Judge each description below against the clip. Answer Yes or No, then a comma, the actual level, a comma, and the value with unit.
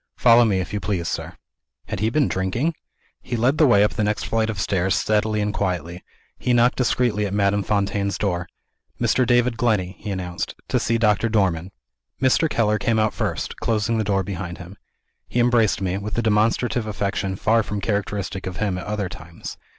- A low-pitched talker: Yes, low, 105 Hz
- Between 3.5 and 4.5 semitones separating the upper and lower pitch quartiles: No, average, 3.1 semitones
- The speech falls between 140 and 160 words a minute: No, average, 195 wpm